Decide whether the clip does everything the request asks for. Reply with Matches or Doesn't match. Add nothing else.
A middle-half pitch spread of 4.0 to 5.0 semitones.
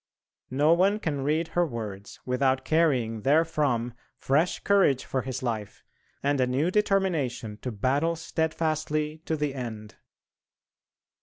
Matches